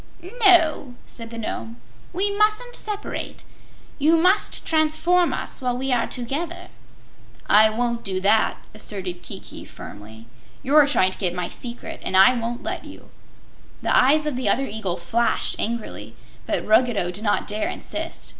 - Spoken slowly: No, average, 155 wpm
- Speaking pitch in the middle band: No, high, 240 Hz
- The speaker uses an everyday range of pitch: No, wide, 6.8 semitones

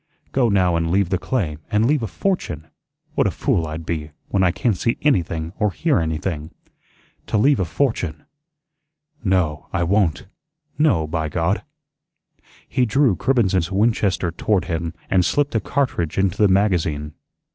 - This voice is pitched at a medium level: No, very low, 95 Hz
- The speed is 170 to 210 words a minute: No, average, 155 wpm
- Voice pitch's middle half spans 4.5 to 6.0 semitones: Yes, average, 5.1 semitones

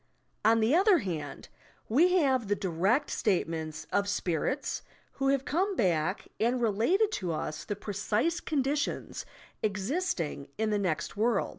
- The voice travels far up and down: Yes, wide, 7.1 semitones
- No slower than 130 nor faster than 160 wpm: Yes, average, 145 wpm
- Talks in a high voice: Yes, high, 220 Hz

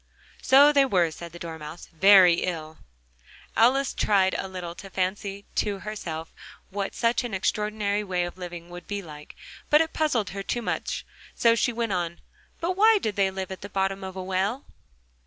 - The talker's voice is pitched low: No, high, 195 Hz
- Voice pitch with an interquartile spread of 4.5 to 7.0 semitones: No, average, 3.8 semitones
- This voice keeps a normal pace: Yes, average, 185 wpm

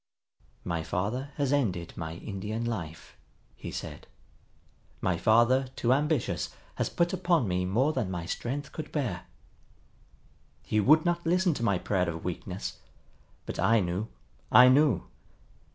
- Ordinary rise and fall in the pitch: No, wide, 7.8 semitones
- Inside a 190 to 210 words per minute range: No, average, 140 wpm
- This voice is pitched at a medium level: No, low, 115 Hz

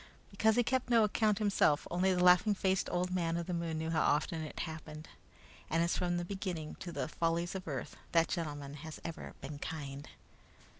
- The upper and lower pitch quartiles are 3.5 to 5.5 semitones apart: No, average, 3.1 semitones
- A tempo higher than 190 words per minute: Yes, average, 200 wpm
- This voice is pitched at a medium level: Yes, medium, 170 Hz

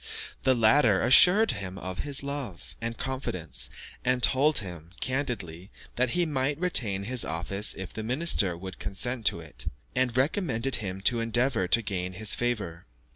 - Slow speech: No, average, 160 wpm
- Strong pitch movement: Yes, wide, 5.9 semitones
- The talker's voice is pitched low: Yes, low, 115 Hz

